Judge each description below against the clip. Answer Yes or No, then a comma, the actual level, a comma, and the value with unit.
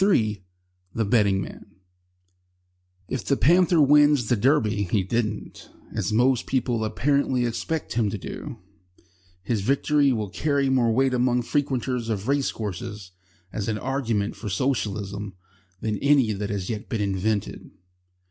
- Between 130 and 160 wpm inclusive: Yes, average, 140 wpm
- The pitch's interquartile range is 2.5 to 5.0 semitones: Yes, average, 4.4 semitones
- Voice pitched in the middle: No, low, 115 Hz